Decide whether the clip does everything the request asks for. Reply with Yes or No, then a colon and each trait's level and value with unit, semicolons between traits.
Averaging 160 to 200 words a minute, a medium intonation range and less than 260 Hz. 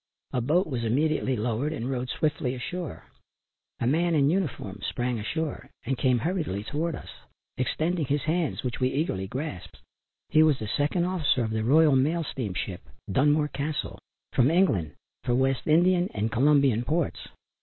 Yes: average, 165 wpm; average, 4.6 semitones; medium, 140 Hz